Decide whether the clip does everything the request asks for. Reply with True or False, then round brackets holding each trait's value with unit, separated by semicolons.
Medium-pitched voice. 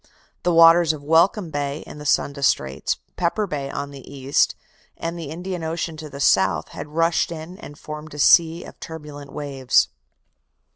True (155 Hz)